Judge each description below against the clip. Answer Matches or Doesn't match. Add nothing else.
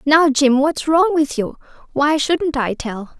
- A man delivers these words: Doesn't match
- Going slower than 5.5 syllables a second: Matches